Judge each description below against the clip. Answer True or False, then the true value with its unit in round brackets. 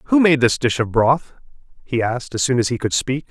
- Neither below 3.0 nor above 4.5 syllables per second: False (5.4 syllables/s)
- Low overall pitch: True (130 Hz)